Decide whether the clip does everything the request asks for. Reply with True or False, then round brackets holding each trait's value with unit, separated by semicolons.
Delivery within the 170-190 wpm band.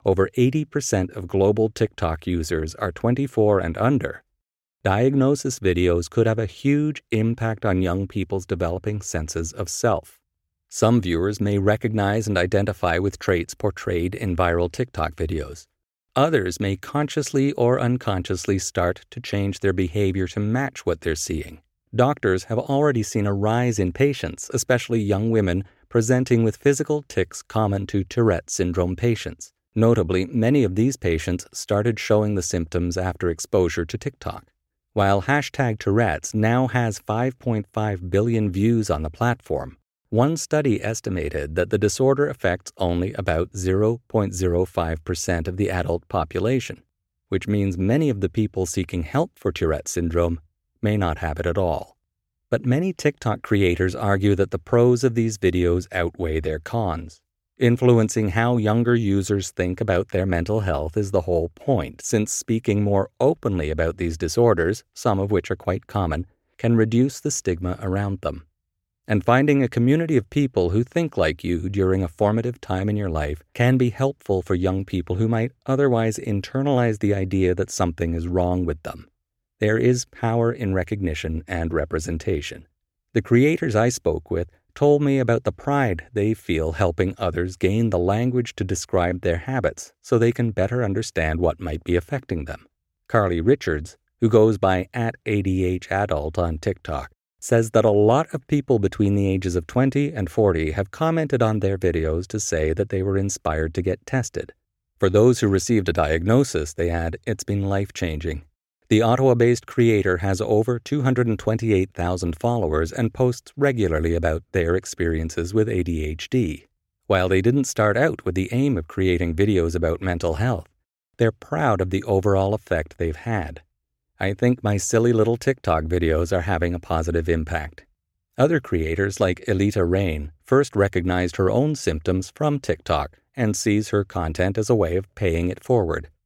False (160 wpm)